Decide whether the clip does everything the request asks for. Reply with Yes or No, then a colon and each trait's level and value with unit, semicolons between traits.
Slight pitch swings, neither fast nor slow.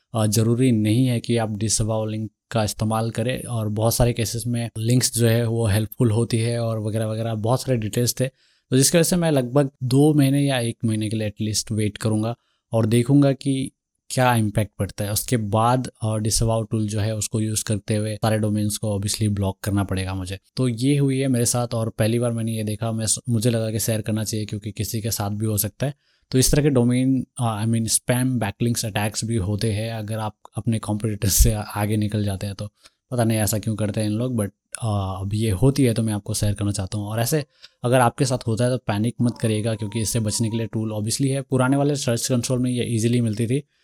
No: narrow, 2.3 semitones; fast, 230 wpm